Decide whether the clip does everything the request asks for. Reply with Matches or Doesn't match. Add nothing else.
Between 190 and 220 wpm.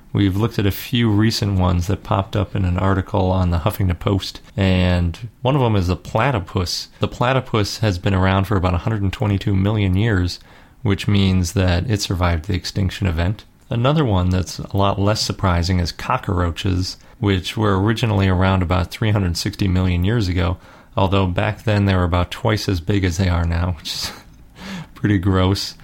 Doesn't match